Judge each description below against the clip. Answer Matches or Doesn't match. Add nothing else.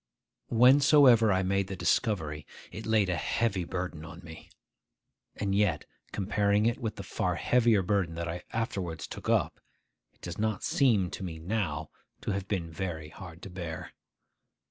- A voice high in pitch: Doesn't match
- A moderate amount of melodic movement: Matches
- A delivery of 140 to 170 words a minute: Matches